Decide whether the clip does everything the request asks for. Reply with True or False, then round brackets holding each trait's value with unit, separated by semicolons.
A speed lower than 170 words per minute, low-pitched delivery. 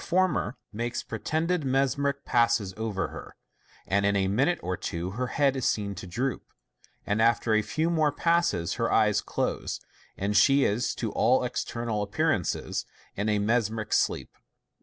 True (160 wpm; 115 Hz)